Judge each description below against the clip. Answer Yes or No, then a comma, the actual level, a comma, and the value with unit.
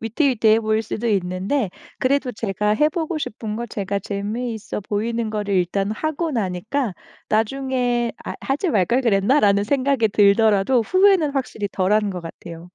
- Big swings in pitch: No, average, 4.6 semitones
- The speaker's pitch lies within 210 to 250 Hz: Yes, high, 220 Hz